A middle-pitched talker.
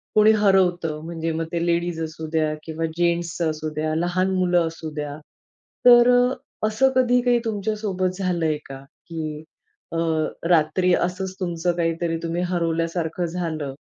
Yes: medium, 170 Hz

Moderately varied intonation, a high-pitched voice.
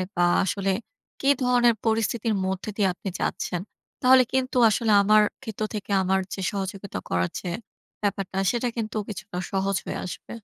Yes: average, 3.1 semitones; high, 205 Hz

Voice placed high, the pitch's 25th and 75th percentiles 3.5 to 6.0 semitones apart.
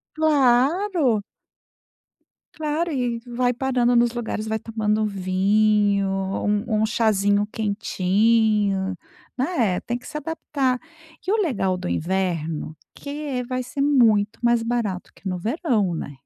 Yes: high, 225 Hz; average, 4.2 semitones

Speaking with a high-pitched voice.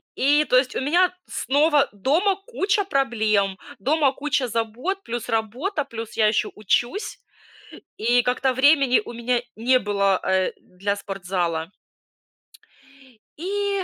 Yes: very high, 250 Hz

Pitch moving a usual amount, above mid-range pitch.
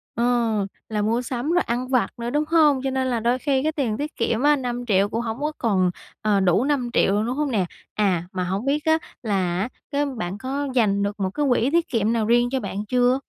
Yes: average, 4.5 semitones; high, 240 Hz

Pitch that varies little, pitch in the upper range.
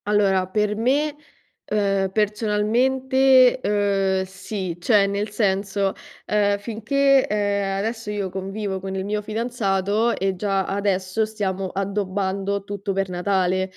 Yes: narrow, 1.8 semitones; high, 200 Hz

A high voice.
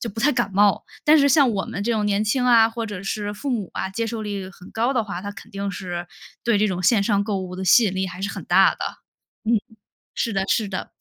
Yes: high, 205 Hz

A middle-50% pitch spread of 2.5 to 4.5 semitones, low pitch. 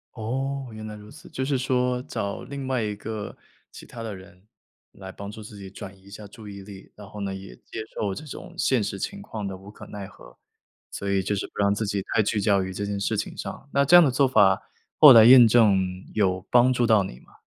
Yes: average, 3.9 semitones; low, 105 Hz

